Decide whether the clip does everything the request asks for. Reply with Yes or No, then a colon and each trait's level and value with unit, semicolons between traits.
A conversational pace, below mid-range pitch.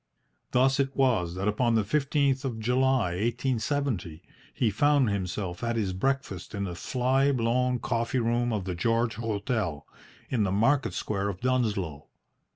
Yes: average, 155 wpm; low, 115 Hz